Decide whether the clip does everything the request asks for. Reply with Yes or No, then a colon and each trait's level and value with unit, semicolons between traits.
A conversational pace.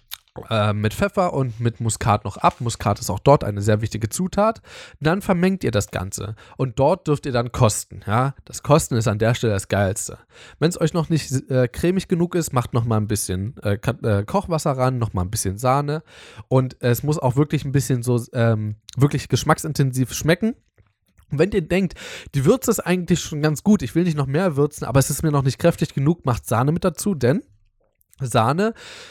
No: fast, 210 wpm